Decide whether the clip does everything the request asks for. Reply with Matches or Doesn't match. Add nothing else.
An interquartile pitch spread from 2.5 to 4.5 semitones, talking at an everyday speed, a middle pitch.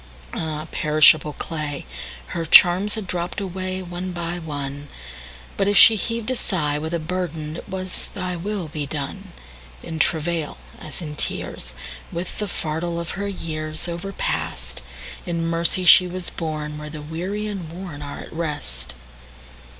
Doesn't match